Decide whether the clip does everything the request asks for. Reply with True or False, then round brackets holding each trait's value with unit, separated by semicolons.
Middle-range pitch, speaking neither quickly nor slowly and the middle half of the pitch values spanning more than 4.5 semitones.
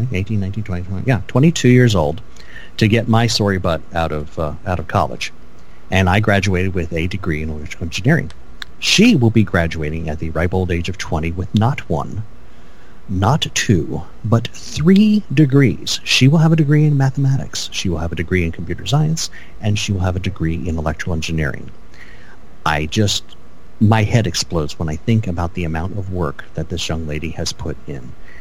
False (95 Hz; 190 wpm; 5.6 semitones)